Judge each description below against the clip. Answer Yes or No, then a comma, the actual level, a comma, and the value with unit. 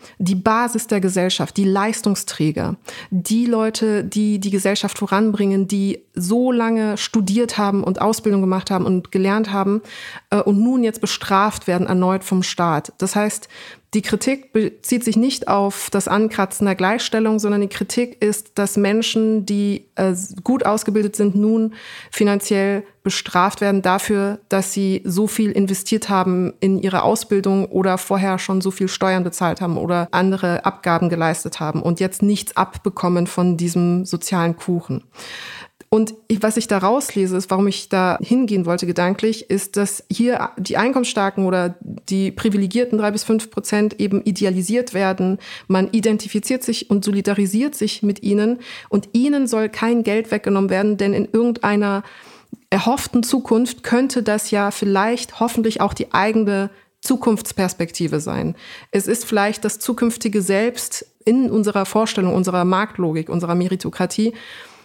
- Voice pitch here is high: Yes, high, 205 Hz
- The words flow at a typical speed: Yes, average, 145 wpm